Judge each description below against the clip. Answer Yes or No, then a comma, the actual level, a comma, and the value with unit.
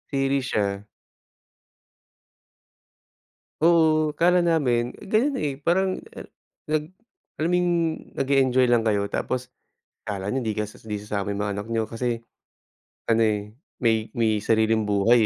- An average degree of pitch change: No, wide, 6.0 semitones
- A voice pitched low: Yes, low, 120 Hz